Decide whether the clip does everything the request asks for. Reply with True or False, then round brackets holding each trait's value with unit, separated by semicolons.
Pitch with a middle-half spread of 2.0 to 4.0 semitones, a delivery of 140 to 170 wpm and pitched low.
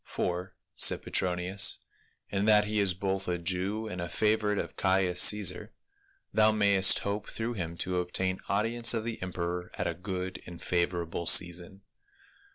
True (2.8 semitones; 160 wpm; 95 Hz)